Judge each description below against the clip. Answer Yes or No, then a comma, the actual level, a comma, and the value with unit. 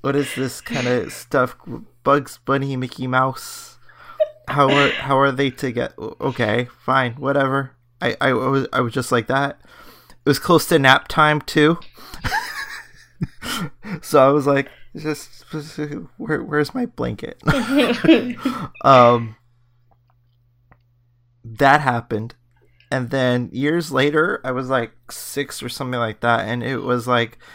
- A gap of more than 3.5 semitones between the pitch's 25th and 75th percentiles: No, average, 3.1 semitones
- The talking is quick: No, average, 140 wpm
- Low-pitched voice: Yes, low, 130 Hz